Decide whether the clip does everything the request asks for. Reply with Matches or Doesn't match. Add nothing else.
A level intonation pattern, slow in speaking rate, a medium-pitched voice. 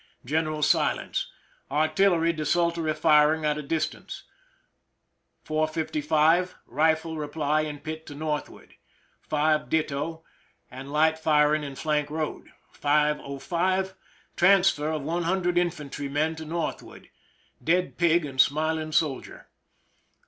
Matches